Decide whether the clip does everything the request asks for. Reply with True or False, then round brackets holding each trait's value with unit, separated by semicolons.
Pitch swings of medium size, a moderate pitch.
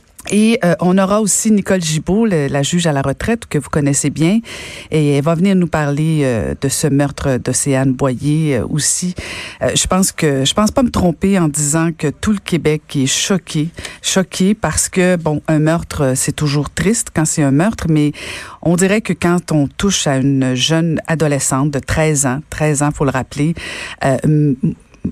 True (4.1 semitones; 155 Hz)